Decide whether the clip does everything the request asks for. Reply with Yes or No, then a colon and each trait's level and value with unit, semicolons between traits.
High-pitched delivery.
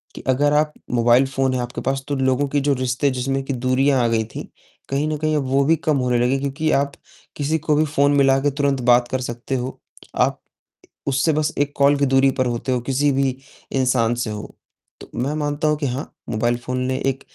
No: low, 135 Hz